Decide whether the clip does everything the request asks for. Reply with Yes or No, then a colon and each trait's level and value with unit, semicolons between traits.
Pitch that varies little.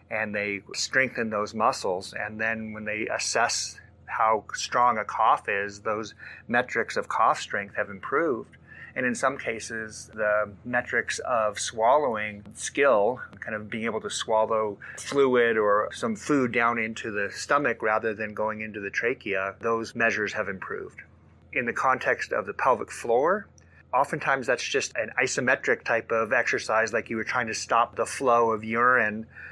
Yes: narrow, 1.4 semitones